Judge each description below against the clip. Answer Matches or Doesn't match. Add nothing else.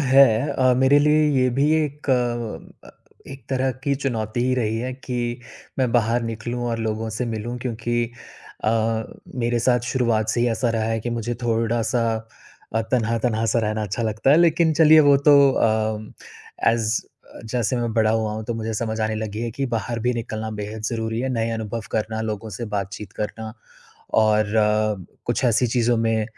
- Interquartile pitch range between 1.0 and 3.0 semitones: Matches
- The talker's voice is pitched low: Matches